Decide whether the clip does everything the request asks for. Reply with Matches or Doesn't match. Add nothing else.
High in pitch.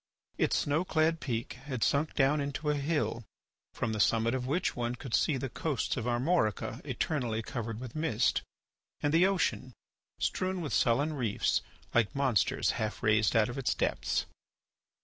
Doesn't match